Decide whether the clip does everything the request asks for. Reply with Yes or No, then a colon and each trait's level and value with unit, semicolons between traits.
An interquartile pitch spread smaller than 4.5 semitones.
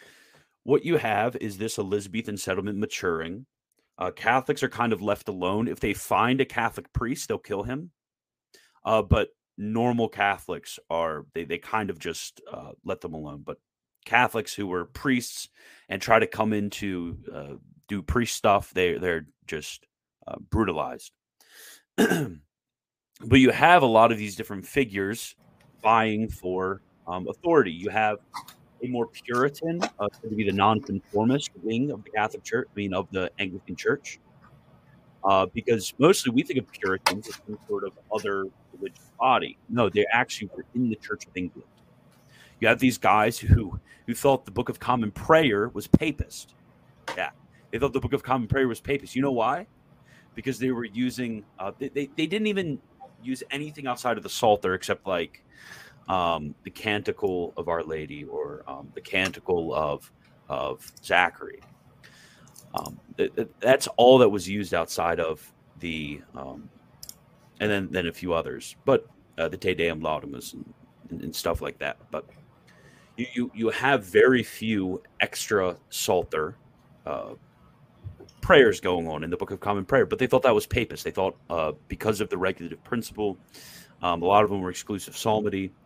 No: average, 4.9 semitones